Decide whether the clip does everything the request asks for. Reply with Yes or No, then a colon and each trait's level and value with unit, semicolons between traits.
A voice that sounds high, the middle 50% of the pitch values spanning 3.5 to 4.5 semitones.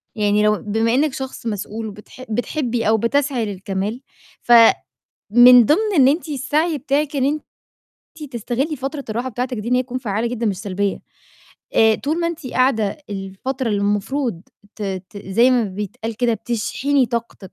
Yes: high, 235 Hz; average, 4.2 semitones